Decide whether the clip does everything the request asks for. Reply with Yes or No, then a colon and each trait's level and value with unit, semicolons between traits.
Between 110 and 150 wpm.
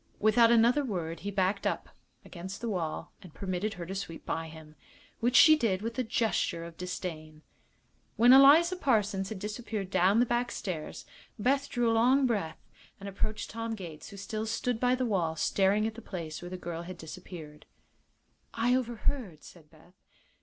No: average, 180 wpm